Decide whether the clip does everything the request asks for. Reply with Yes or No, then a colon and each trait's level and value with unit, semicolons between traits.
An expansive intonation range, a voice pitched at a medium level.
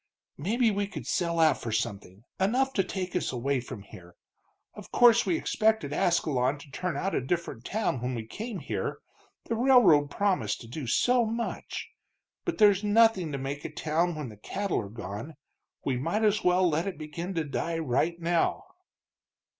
Yes: wide, 7.4 semitones; medium, 170 Hz